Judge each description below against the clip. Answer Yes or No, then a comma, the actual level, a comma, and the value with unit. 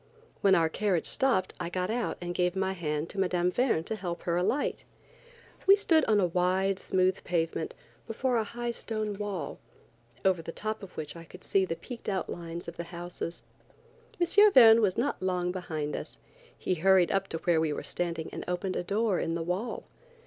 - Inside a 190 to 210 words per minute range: Yes, average, 195 wpm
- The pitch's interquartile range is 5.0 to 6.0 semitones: No, average, 3.7 semitones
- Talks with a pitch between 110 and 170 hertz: No, medium, 185 Hz